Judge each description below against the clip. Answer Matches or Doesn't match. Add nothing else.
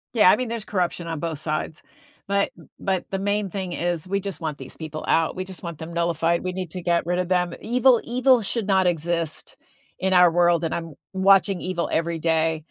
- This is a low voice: Doesn't match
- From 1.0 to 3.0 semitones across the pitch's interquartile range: Matches